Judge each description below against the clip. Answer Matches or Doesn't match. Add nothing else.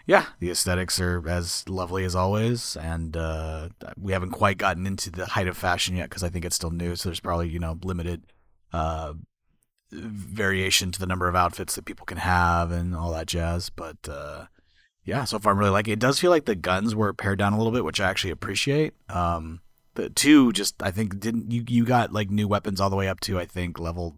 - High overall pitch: Doesn't match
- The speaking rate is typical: Doesn't match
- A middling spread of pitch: Matches